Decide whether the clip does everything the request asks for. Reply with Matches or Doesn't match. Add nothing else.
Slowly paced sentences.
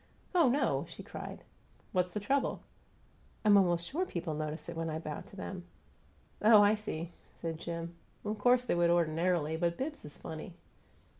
Doesn't match